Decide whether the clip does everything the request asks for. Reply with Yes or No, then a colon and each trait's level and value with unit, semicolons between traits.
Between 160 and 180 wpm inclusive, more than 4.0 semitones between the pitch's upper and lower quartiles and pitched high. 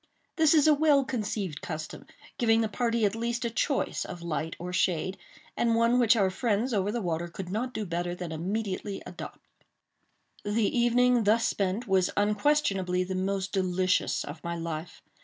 Yes: average, 175 wpm; average, 4.6 semitones; high, 205 Hz